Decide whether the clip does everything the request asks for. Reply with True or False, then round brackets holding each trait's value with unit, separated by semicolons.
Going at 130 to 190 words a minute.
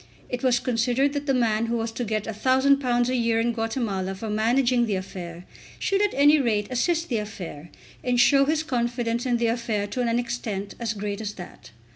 False (200 wpm)